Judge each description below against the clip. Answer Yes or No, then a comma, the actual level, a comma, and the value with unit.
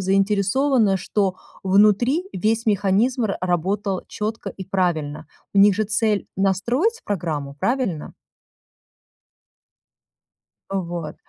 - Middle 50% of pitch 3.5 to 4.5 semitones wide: No, average, 3.0 semitones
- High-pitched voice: Yes, high, 195 Hz